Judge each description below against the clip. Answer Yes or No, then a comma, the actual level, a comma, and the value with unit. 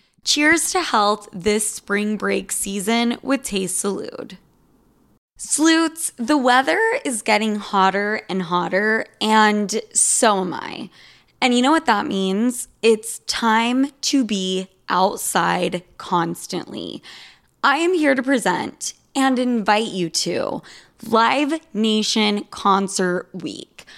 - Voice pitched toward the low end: No, high, 220 Hz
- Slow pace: Yes, slow, 120 wpm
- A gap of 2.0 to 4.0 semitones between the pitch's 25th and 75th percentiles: No, average, 4.6 semitones